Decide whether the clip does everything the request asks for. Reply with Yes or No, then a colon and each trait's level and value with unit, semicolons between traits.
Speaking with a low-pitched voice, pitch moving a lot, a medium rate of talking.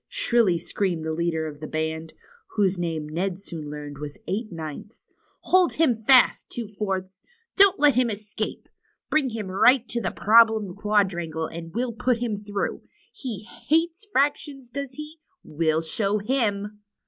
No: high, 205 Hz; wide, 6.5 semitones; average, 160 wpm